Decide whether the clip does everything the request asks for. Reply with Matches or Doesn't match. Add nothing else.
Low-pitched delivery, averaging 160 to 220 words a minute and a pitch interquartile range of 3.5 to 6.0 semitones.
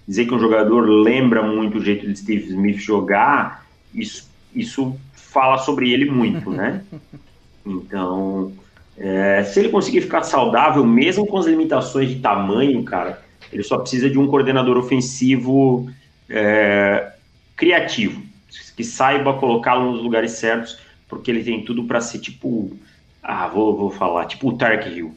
Doesn't match